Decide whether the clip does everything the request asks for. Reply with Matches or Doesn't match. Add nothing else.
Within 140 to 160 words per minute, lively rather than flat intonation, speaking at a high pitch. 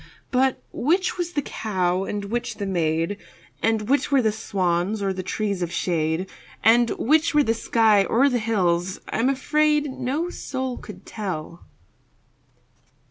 Matches